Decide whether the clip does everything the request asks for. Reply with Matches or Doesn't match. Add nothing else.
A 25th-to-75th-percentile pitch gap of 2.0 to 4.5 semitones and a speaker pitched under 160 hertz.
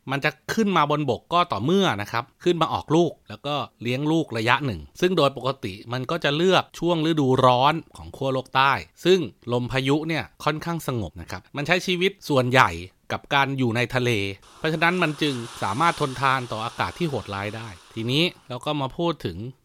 Doesn't match